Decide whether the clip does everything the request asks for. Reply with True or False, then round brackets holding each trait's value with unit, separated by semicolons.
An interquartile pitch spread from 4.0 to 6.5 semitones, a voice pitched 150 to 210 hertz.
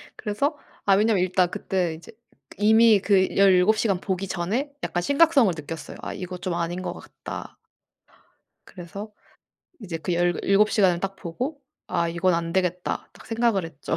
False (3.4 semitones; 190 Hz)